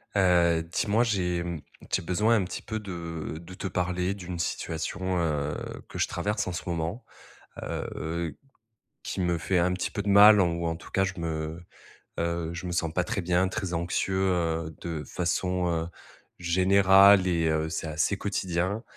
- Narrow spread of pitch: Yes, narrow, 2.2 semitones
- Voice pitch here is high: No, very low, 90 Hz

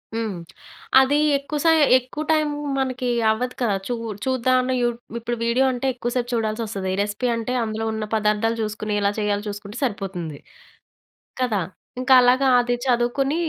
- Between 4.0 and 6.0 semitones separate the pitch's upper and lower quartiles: No, average, 3.2 semitones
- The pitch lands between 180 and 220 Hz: No, high, 240 Hz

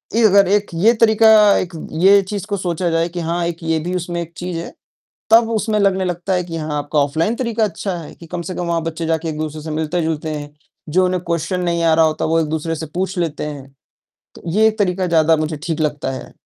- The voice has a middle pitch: Yes, medium, 170 Hz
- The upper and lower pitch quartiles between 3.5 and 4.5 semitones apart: No, average, 2.8 semitones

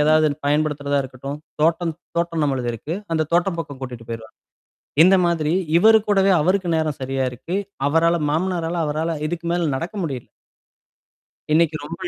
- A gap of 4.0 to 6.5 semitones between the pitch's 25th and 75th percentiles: No, average, 3.2 semitones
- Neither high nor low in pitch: Yes, medium, 155 Hz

